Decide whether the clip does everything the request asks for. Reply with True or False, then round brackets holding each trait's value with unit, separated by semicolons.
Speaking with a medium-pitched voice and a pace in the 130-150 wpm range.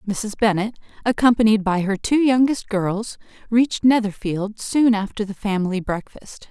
False (215 Hz; 140 wpm)